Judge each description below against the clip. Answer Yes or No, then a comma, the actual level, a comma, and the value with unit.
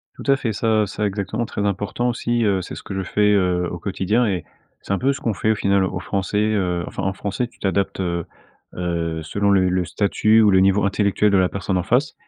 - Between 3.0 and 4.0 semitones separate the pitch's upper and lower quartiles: No, narrow, 2.5 semitones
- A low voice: Yes, low, 100 Hz